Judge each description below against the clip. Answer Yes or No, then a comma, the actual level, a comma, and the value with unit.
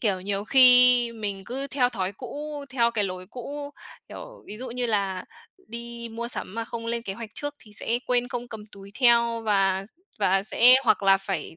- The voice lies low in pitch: No, high, 230 Hz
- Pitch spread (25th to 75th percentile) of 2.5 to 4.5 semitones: Yes, average, 3.7 semitones